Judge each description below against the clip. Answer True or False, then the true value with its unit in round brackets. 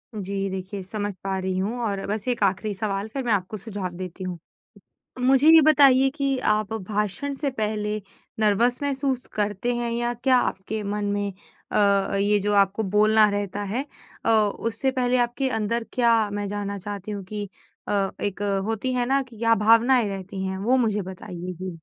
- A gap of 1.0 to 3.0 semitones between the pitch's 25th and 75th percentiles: False (3.4 semitones)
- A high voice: True (210 Hz)